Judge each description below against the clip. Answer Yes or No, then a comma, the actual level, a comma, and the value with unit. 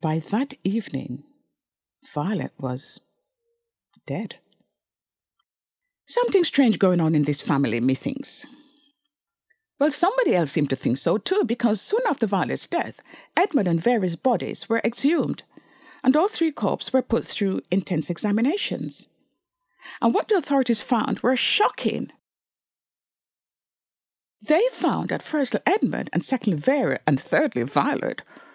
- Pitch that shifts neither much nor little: No, wide, 8.9 semitones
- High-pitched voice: Yes, very high, 260 Hz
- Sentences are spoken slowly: Yes, slow, 125 wpm